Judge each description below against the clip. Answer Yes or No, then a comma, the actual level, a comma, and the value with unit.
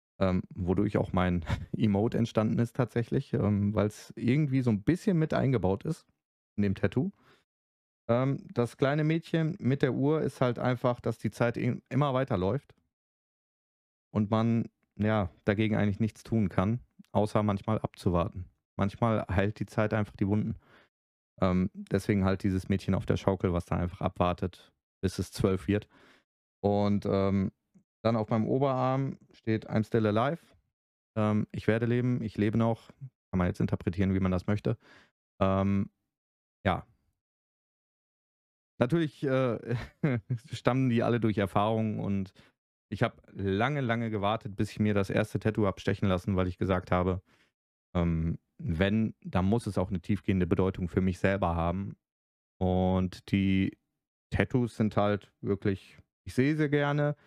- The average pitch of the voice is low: Yes, low, 105 Hz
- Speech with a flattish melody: No, average, 3.8 semitones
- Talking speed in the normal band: Yes, average, 155 wpm